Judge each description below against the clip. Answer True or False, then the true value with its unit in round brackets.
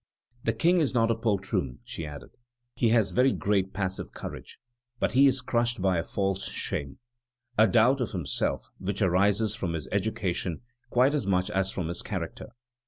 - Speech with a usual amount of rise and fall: True (4.0 semitones)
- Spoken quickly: False (175 wpm)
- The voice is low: True (100 Hz)